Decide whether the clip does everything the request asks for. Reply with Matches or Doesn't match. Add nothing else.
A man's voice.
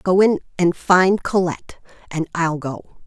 Doesn't match